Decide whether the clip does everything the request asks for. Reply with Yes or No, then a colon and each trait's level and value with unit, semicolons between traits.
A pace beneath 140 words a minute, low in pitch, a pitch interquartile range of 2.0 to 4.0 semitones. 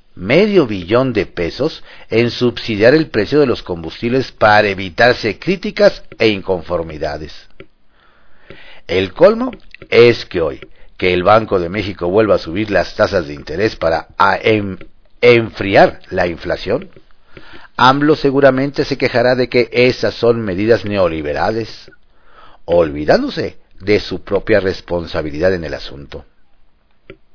No: slow, 125 wpm; low, 110 Hz; average, 5.1 semitones